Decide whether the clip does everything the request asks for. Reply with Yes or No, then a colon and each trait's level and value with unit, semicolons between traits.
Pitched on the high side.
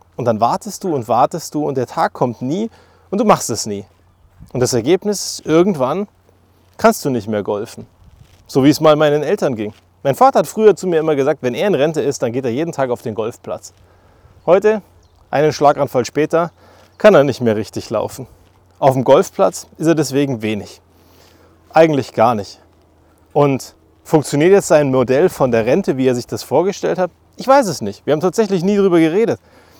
No: low, 130 Hz